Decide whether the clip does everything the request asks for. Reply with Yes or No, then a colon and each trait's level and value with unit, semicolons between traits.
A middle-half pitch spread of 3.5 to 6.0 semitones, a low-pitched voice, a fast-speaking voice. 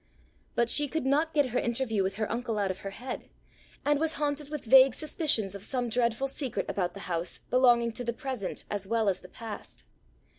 No: average, 4.6 semitones; high, 235 Hz; fast, 210 wpm